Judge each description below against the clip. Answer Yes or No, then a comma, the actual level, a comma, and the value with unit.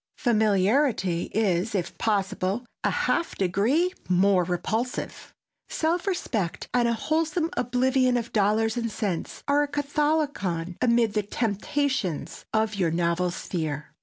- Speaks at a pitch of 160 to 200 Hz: No, high, 220 Hz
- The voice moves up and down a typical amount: No, wide, 6.4 semitones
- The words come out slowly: Yes, slow, 125 wpm